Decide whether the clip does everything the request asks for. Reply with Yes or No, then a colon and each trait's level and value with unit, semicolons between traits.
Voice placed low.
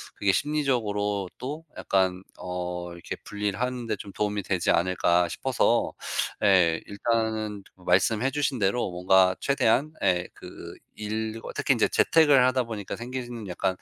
Yes: low, 105 Hz